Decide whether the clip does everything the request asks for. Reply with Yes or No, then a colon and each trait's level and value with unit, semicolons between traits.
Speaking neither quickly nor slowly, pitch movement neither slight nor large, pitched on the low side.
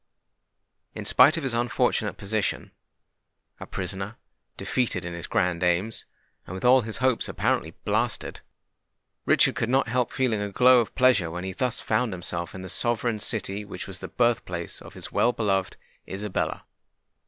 Yes: average, 160 wpm; average, 4.7 semitones; low, 105 Hz